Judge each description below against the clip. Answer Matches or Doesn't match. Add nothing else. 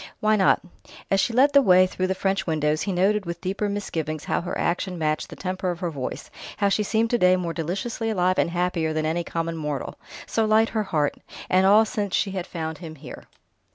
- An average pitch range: Matches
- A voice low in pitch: Doesn't match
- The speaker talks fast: Matches